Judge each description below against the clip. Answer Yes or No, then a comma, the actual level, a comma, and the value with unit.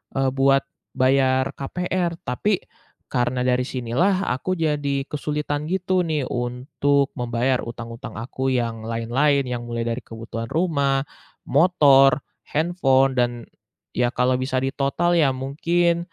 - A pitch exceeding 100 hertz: Yes, low, 135 Hz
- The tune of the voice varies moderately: Yes, average, 3.5 semitones